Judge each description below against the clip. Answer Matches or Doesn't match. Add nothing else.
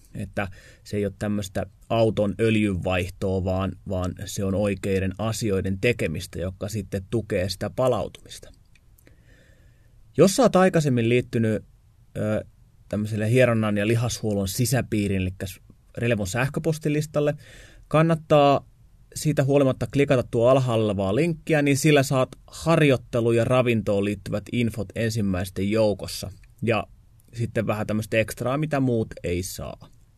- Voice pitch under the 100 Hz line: Doesn't match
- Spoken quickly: Doesn't match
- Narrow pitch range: Doesn't match